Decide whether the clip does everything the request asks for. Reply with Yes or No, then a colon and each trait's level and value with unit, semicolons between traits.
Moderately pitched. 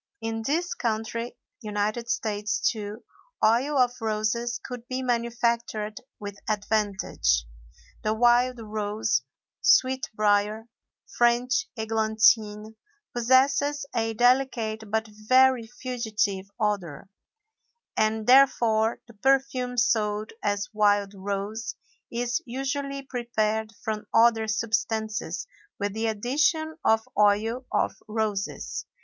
No: high, 220 Hz